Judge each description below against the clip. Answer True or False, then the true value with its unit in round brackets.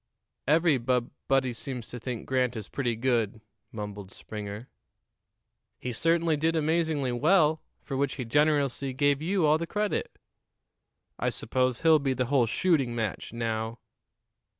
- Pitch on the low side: True (130 Hz)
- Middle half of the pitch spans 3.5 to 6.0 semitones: True (4.7 semitones)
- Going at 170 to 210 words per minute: False (145 wpm)